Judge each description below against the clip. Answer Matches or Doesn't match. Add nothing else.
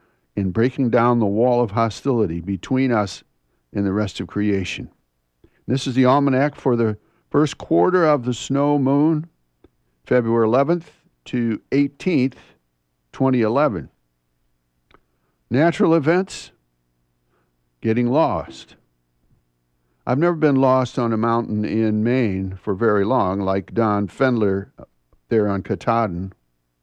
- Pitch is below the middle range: Matches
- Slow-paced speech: Matches